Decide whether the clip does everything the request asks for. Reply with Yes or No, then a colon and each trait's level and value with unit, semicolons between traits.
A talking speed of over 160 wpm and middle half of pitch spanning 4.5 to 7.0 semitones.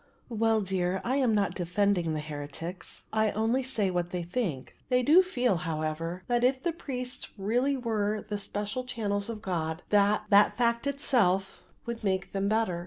Yes: average, 175 wpm; average, 5.1 semitones